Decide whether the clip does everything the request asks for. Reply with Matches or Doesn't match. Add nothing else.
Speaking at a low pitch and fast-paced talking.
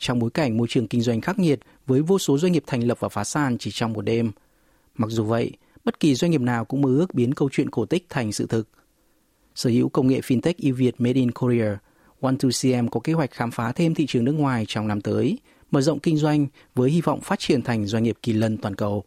Matches